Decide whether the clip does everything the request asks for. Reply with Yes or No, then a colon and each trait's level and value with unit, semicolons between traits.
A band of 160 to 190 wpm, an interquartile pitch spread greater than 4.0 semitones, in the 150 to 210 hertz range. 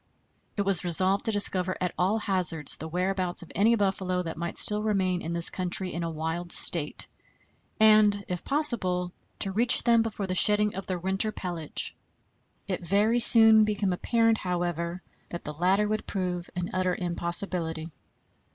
No: average, 165 wpm; average, 3.1 semitones; medium, 185 Hz